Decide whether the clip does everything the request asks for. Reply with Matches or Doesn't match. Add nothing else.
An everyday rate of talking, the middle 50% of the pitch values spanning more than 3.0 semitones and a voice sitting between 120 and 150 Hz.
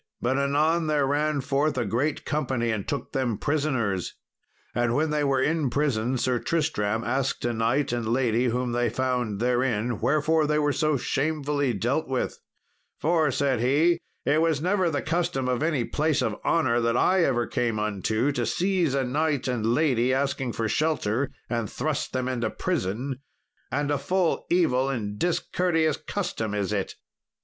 Matches